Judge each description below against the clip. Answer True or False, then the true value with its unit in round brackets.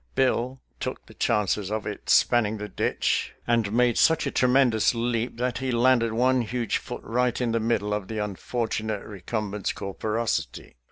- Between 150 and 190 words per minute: True (170 wpm)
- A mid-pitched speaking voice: False (115 Hz)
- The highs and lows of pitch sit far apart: False (2.8 semitones)